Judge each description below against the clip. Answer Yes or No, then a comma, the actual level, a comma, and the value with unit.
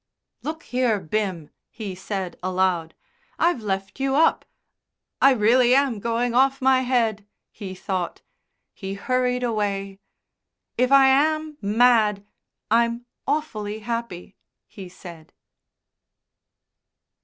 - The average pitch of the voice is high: Yes, high, 225 Hz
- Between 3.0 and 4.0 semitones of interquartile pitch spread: No, average, 4.7 semitones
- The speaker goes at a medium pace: No, slow, 110 wpm